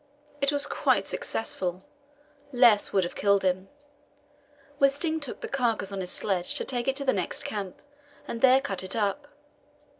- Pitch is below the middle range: No, high, 225 Hz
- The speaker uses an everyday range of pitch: No, wide, 6.2 semitones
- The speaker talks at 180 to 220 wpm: No, average, 170 wpm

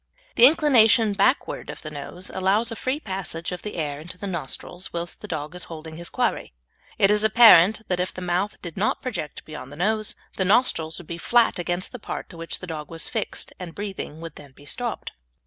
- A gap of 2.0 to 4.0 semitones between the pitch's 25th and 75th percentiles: No, average, 4.5 semitones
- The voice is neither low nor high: Yes, medium, 180 Hz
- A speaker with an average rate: No, fast, 215 wpm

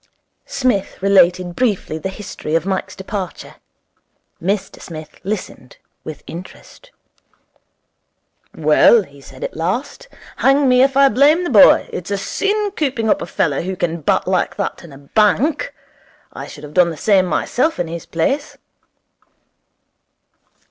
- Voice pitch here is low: No, high, 190 Hz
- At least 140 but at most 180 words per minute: Yes, average, 145 wpm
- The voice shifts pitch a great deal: Yes, wide, 7.5 semitones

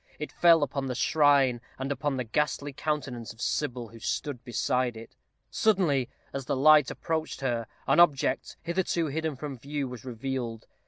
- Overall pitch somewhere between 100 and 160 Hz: Yes, low, 135 Hz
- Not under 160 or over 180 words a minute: Yes, average, 165 wpm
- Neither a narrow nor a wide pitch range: Yes, average, 3.3 semitones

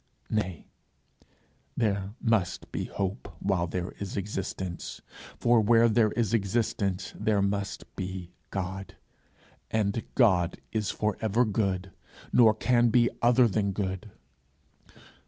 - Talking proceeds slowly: Yes, slow, 120 wpm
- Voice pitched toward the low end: Yes, low, 100 Hz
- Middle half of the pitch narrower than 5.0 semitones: Yes, average, 2.9 semitones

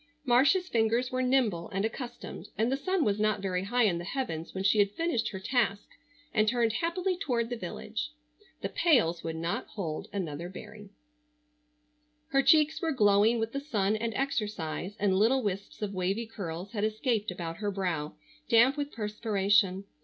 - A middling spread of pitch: Yes, average, 4.5 semitones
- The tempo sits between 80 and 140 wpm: No, average, 175 wpm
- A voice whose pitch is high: Yes, high, 215 Hz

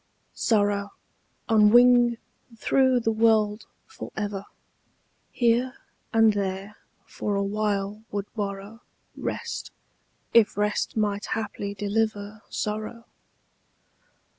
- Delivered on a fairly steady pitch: Yes, narrow, 1.9 semitones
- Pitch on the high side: Yes, high, 215 Hz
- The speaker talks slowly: Yes, slow, 90 wpm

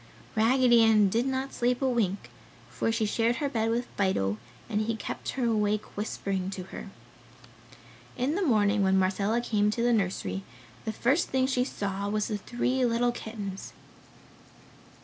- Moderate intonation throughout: Yes, average, 3.3 semitones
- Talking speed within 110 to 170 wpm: Yes, average, 165 wpm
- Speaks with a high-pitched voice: Yes, high, 220 Hz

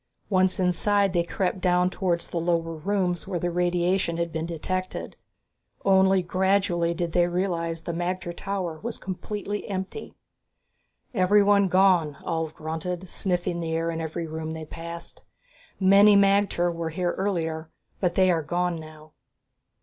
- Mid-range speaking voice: Yes, medium, 175 Hz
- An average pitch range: No, narrow, 2.2 semitones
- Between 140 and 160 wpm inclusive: Yes, average, 150 wpm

